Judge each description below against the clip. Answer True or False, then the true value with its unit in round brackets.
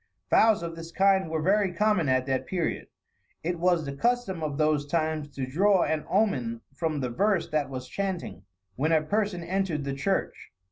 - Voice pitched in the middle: True (165 Hz)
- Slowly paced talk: False (185 wpm)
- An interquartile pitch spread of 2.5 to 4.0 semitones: False (5.0 semitones)